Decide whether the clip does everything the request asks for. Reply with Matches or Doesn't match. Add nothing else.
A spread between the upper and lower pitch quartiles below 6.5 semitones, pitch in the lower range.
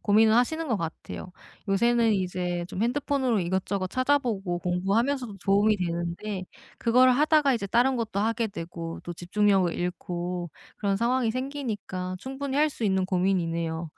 Doesn't match